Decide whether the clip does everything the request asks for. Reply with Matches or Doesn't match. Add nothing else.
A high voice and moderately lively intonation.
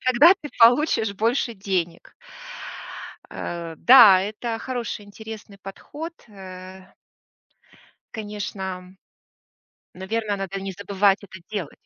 Matches